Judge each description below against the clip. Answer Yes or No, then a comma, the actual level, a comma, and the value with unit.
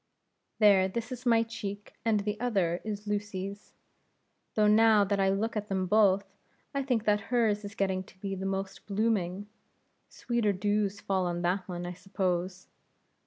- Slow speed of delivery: No, average, 165 wpm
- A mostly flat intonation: Yes, narrow, 2.1 semitones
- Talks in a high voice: Yes, high, 200 Hz